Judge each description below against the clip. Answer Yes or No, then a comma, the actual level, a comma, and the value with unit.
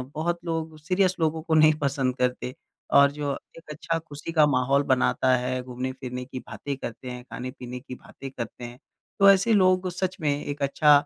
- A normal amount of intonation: Yes, average, 4.2 semitones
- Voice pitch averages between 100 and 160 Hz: Yes, medium, 140 Hz